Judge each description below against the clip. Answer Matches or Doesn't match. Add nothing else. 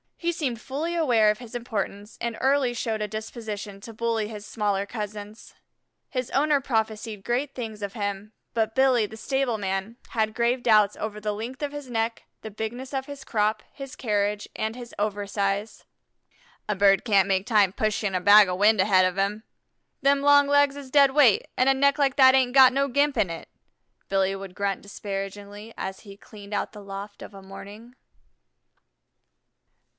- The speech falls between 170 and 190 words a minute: Matches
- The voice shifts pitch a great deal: Doesn't match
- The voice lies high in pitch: Matches